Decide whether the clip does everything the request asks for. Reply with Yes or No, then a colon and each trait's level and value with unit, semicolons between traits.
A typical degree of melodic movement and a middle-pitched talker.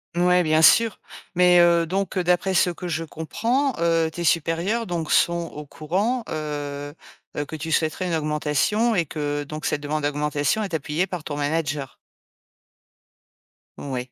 Yes: average, 3.2 semitones; medium, 165 Hz